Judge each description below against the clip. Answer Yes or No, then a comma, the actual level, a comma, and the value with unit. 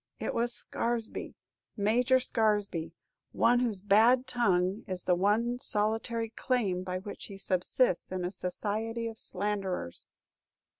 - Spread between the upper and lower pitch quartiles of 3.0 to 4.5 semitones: Yes, average, 3.8 semitones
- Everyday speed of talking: No, slow, 130 wpm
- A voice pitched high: Yes, high, 210 Hz